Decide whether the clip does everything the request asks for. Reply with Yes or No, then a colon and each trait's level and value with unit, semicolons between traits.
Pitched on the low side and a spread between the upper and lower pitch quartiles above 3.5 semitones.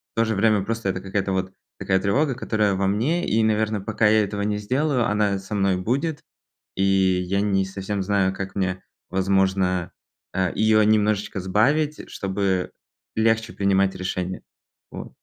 No: low, 100 Hz; narrow, 2.4 semitones